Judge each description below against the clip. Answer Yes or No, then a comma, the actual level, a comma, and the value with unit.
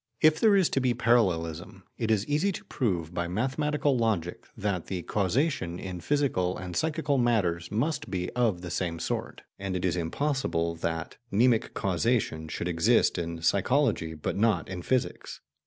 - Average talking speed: Yes, average, 165 wpm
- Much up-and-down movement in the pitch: Yes, wide, 6.9 semitones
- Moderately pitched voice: No, low, 100 Hz